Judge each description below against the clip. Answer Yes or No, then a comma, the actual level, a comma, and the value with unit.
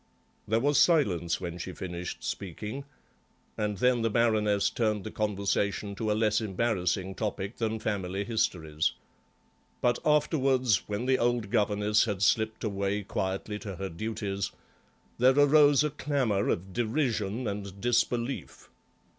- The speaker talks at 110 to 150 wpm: Yes, slow, 135 wpm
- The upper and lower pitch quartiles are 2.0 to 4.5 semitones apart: Yes, average, 3.5 semitones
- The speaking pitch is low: Yes, low, 105 Hz